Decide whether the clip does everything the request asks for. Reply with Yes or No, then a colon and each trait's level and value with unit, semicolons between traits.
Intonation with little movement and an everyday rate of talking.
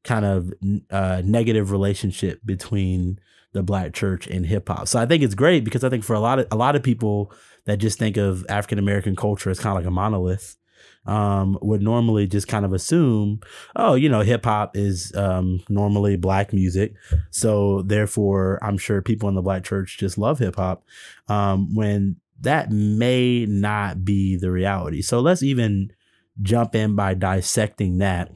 Yes: narrow, 2.3 semitones; average, 185 wpm